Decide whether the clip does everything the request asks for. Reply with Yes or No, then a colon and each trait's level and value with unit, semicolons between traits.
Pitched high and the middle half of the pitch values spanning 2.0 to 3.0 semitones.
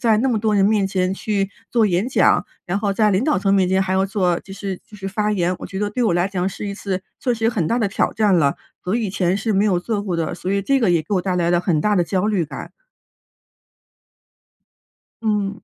Yes: high, 195 Hz; narrow, 2.5 semitones